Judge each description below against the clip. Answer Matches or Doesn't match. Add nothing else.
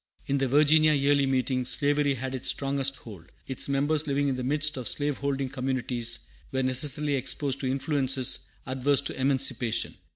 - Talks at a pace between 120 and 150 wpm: Doesn't match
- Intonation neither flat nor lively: Doesn't match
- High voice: Doesn't match